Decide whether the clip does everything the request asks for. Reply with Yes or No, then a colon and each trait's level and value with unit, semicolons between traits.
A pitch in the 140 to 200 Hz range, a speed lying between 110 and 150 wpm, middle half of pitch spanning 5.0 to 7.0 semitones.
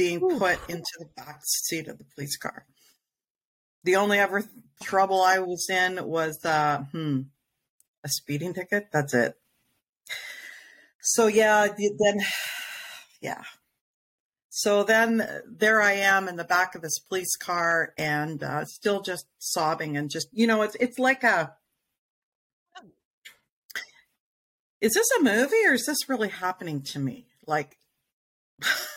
Yes: medium, 185 Hz; average, 140 wpm; wide, 5.6 semitones